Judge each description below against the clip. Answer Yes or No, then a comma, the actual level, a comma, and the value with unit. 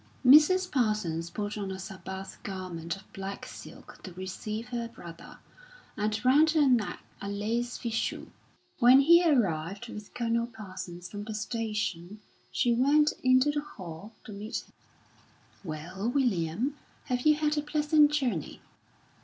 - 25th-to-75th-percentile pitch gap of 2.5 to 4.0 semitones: No, wide, 5.4 semitones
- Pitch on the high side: Yes, high, 220 Hz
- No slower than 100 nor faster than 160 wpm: Yes, average, 145 wpm